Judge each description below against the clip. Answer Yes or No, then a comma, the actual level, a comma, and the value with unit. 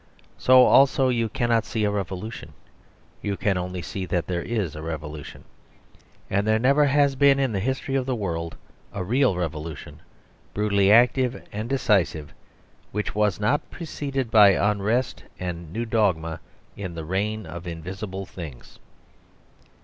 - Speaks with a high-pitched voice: No, low, 105 Hz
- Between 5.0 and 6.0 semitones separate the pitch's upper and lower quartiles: Yes, wide, 5.4 semitones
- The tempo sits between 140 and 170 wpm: Yes, average, 150 wpm